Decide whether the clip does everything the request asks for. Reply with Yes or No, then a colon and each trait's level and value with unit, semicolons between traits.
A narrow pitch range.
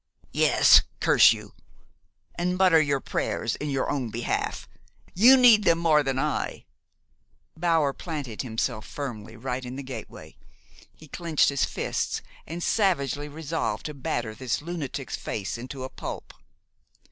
No: average, 4.6 semitones